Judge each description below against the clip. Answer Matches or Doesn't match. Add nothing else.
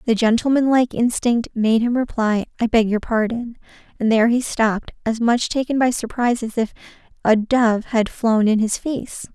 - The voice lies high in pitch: Matches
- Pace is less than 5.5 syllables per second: Matches